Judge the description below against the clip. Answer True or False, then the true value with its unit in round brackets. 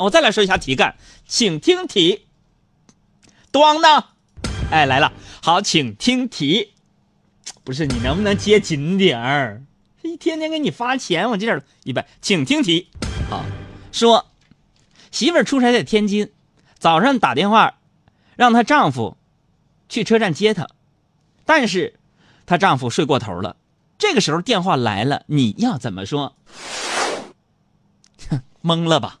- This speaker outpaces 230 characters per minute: False (200 characters per minute)